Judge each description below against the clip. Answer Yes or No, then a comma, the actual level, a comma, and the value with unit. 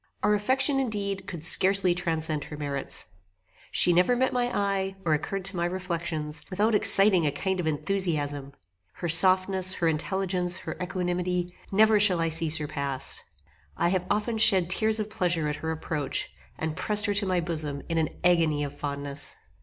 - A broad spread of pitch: No, average, 3.8 semitones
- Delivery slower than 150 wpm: No, average, 170 wpm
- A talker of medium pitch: Yes, medium, 180 Hz